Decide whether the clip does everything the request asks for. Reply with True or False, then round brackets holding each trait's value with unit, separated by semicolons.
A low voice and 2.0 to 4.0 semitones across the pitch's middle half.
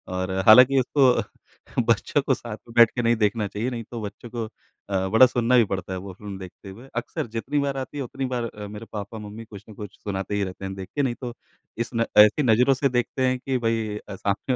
True (115 Hz; 3.5 semitones)